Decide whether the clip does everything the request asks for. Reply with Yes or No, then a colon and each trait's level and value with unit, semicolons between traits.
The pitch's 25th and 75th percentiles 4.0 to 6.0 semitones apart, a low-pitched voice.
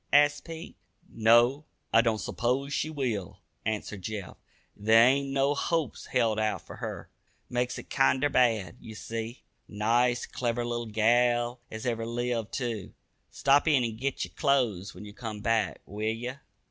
No: average, 3.2 semitones; low, 120 Hz